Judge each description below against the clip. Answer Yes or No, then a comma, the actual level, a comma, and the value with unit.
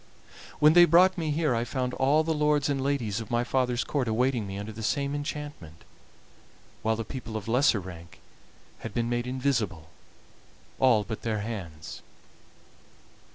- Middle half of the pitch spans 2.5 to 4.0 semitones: No, average, 4.7 semitones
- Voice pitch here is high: No, low, 120 Hz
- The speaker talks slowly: No, average, 160 wpm